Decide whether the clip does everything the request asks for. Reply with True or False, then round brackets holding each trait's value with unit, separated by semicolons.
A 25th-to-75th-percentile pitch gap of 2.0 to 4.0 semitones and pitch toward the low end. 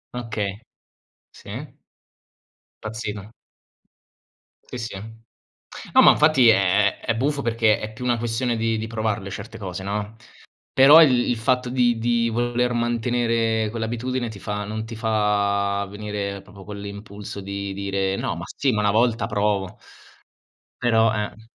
True (2.7 semitones; 110 Hz)